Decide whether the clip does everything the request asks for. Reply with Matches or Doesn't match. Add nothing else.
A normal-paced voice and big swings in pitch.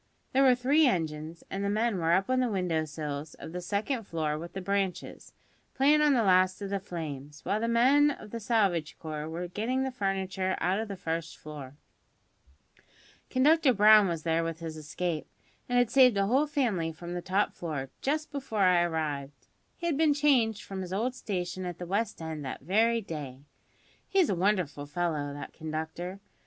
Matches